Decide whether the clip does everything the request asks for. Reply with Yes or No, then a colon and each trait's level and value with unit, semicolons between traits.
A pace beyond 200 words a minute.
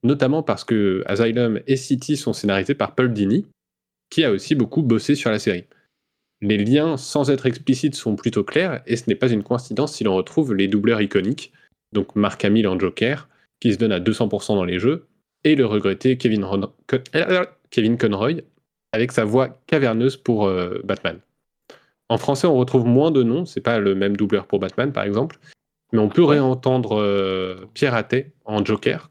No: average, 195 wpm